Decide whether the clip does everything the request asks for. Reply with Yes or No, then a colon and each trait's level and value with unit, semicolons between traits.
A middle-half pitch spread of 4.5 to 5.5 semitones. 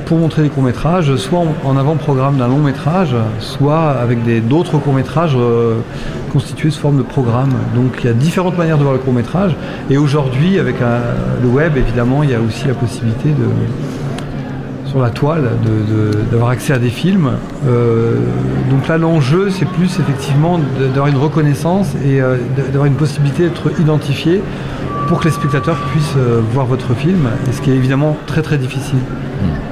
No: average, 3.7 semitones